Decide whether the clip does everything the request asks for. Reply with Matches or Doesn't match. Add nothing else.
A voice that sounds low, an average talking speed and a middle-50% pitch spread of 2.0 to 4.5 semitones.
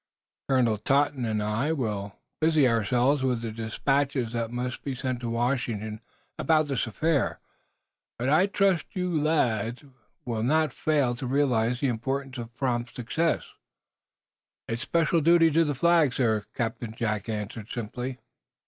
Matches